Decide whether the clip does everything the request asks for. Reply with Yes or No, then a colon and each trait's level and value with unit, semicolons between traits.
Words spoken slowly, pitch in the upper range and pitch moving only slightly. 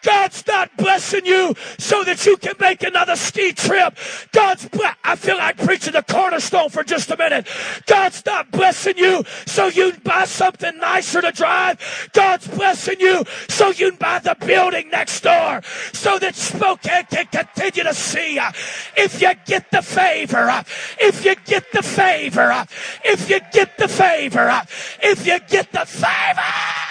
No: average, 175 wpm; very high, 370 Hz; narrow, 2.1 semitones